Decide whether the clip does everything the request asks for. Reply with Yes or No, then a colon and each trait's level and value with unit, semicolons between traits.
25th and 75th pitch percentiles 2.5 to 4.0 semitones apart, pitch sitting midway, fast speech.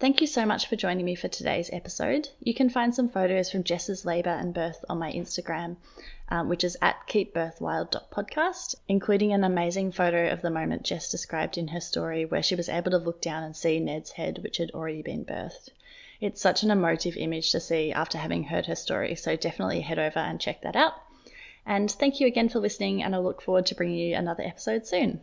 Yes: average, 3.7 semitones; medium, 180 Hz; fast, 220 wpm